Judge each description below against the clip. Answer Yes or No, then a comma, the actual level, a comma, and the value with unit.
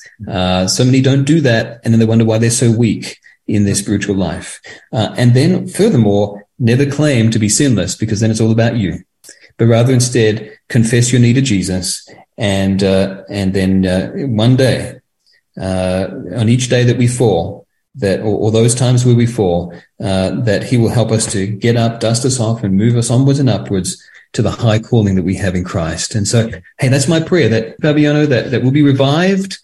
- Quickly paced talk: Yes, fast, 210 wpm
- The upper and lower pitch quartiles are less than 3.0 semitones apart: No, average, 4.0 semitones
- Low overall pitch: Yes, low, 115 Hz